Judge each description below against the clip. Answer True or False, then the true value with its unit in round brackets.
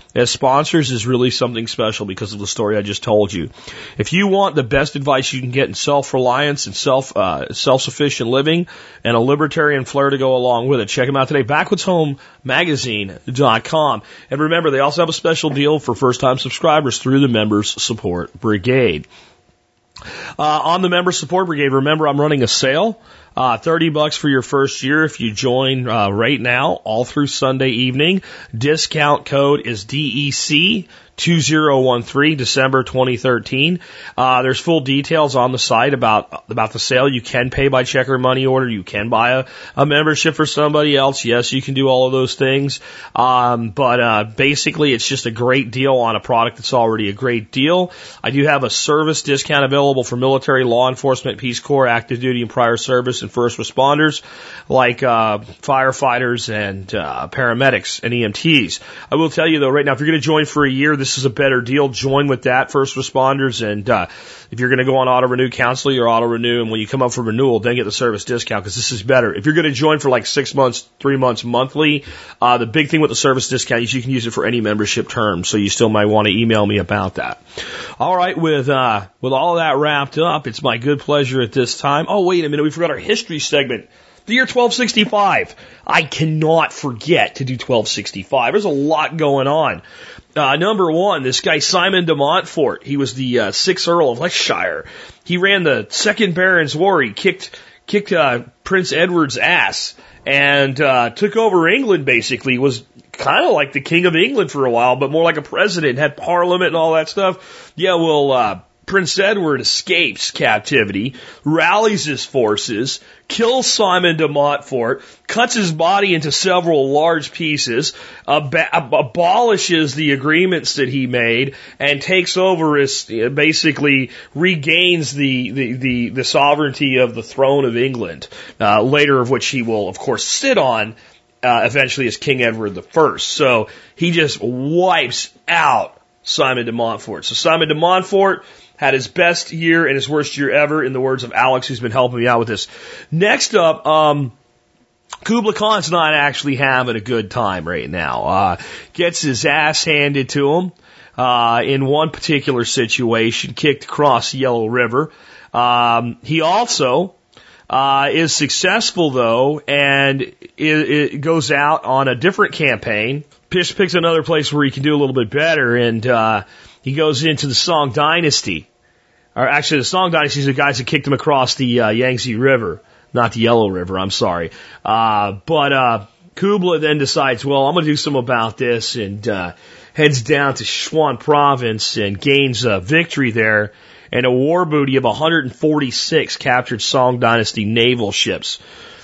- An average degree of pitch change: True (4.1 semitones)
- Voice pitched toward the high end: False (135 Hz)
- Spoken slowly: False (190 wpm)